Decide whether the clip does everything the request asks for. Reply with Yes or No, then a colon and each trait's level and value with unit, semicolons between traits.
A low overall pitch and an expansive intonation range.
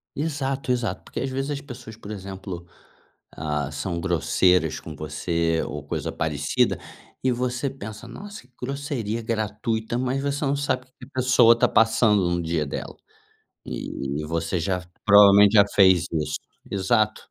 Yes: low, 105 Hz; wide, 6.6 semitones